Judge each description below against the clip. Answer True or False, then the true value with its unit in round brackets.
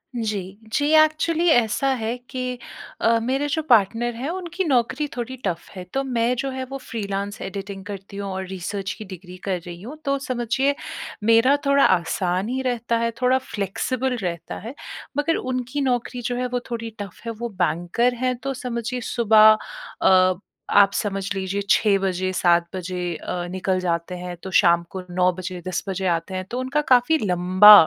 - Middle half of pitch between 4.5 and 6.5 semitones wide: True (5.2 semitones)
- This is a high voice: True (225 Hz)